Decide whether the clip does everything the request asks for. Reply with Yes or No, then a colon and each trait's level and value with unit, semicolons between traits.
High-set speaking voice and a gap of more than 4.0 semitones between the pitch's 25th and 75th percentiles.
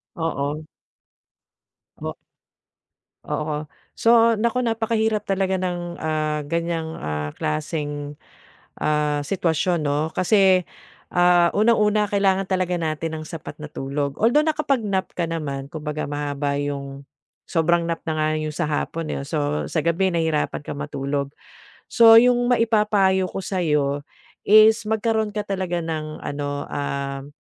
No: medium, 165 Hz; average, 5.2 semitones